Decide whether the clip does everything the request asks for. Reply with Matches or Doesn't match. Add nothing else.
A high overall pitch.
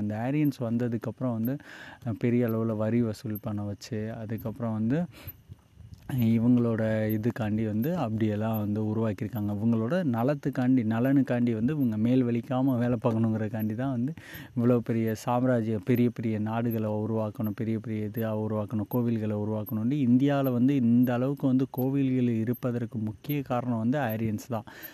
Doesn't match